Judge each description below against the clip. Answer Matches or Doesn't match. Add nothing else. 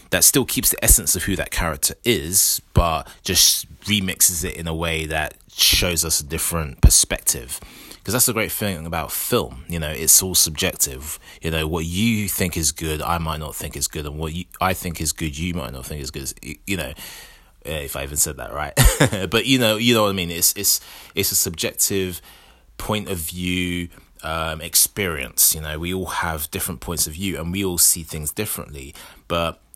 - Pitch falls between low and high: Doesn't match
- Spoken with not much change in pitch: Doesn't match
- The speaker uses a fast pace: Matches